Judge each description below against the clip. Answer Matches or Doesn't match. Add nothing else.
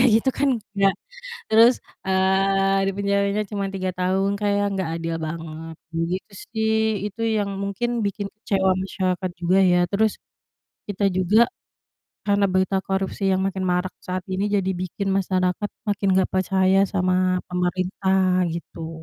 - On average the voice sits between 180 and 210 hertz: Matches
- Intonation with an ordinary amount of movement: Doesn't match